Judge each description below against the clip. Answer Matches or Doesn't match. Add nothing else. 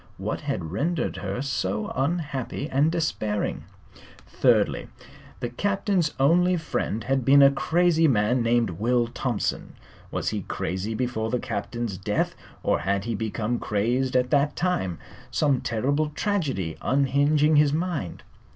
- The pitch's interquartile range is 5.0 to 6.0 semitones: Matches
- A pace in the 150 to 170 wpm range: Doesn't match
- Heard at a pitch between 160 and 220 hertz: Doesn't match